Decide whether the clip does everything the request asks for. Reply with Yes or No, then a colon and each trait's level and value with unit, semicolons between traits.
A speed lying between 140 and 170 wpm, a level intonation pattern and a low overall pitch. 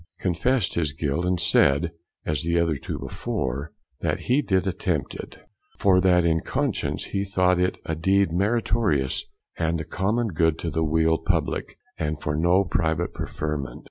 No: average, 165 wpm; average, 3.3 semitones; very low, 85 Hz